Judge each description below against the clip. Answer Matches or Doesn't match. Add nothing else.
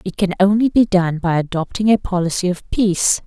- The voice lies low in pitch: Doesn't match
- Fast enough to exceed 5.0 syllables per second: Matches